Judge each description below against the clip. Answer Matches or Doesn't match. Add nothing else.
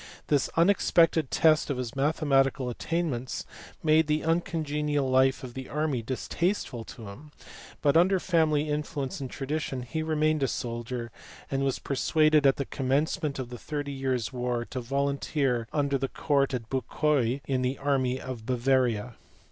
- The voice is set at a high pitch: Doesn't match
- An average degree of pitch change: Matches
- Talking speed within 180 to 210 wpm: Doesn't match